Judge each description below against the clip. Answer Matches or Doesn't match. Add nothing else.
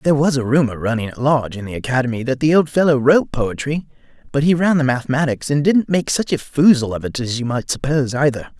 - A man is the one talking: Matches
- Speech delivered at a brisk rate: Matches